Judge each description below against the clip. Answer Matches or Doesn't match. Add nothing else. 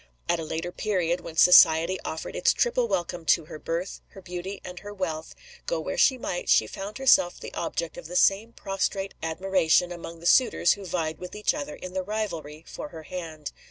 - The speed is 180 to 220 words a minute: Matches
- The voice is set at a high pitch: Doesn't match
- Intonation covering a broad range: Doesn't match